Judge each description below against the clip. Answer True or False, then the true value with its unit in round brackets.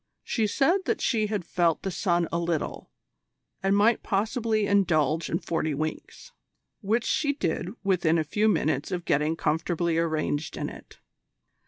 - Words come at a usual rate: True (155 wpm)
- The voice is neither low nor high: True (175 Hz)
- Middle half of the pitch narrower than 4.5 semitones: False (4.8 semitones)